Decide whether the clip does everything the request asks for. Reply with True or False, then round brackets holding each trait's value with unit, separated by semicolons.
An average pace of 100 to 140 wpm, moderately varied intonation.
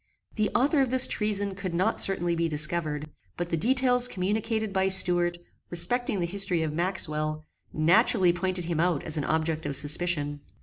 False (170 wpm; 4.1 semitones)